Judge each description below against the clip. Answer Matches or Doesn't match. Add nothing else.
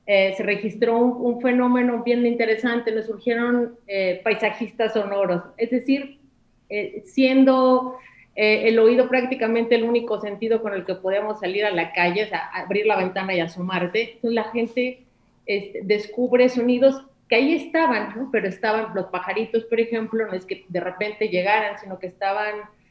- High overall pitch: Matches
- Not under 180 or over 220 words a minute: Doesn't match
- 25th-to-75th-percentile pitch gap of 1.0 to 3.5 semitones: Matches